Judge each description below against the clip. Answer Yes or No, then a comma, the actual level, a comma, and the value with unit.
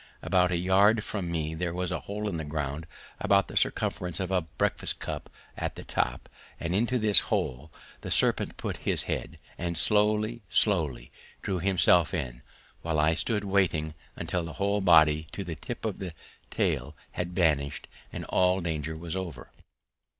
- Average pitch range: Yes, average, 3.7 semitones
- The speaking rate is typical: Yes, average, 170 wpm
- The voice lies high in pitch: No, very low, 90 Hz